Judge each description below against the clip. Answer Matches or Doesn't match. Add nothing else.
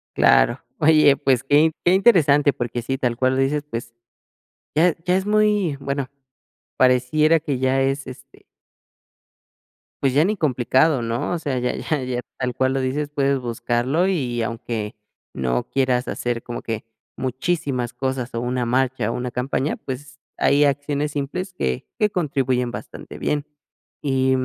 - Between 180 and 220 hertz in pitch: Doesn't match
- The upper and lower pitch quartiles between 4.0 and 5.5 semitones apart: Doesn't match